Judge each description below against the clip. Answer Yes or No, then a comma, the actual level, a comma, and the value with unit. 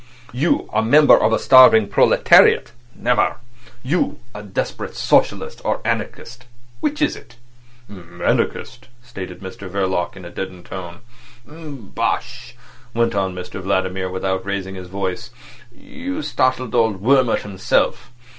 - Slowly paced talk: Yes, slow, 115 wpm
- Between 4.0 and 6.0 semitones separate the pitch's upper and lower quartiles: Yes, average, 4.5 semitones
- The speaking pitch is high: No, low, 105 Hz